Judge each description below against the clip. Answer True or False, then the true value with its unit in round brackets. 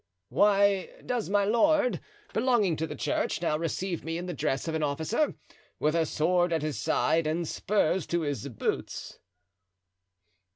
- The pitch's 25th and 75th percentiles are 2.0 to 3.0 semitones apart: False (4.6 semitones)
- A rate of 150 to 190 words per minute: True (160 wpm)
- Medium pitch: True (170 Hz)